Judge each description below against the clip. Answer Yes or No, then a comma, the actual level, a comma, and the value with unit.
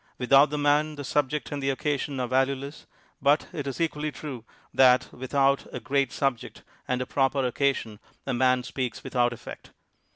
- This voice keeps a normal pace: Yes, average, 175 wpm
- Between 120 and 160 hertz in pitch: Yes, low, 135 Hz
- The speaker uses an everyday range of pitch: No, narrow, 2.1 semitones